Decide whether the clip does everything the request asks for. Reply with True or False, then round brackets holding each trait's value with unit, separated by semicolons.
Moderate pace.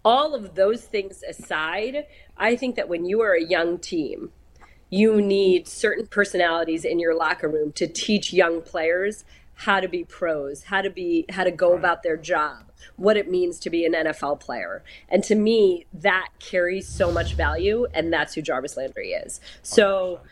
True (185 wpm)